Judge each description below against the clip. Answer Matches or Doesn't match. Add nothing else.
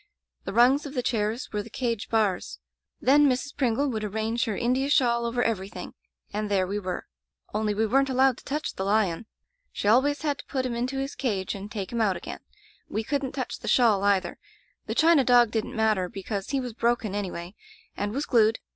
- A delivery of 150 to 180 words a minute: Doesn't match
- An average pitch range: Matches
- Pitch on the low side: Doesn't match